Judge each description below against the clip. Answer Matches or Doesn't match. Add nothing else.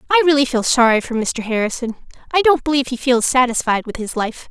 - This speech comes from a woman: Matches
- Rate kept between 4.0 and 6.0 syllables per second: Doesn't match